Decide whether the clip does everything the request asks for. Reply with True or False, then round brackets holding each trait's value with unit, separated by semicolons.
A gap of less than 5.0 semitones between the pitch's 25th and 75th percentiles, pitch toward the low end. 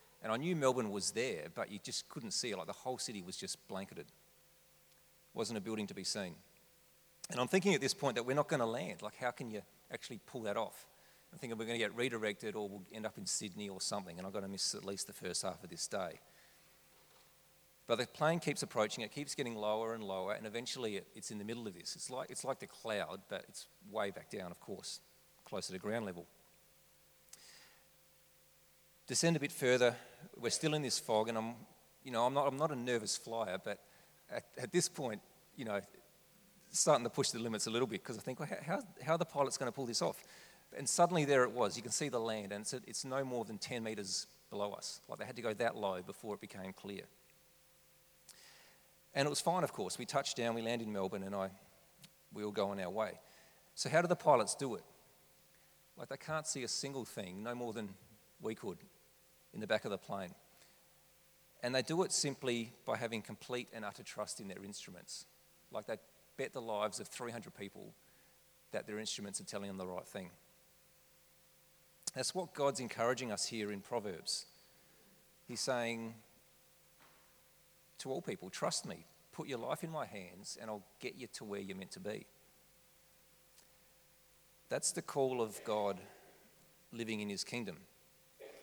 False (5.5 semitones; 120 Hz)